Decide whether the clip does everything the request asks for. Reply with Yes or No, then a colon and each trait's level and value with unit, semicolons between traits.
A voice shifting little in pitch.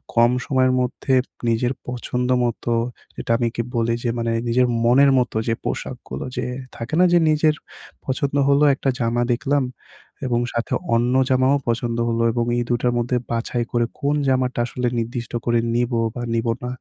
Yes: narrow, 1.7 semitones